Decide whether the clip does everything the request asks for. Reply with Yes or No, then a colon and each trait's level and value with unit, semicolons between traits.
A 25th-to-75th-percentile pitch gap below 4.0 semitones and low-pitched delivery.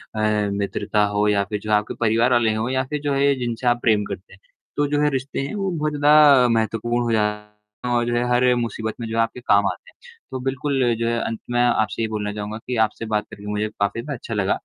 Yes: average, 3.3 semitones; low, 115 Hz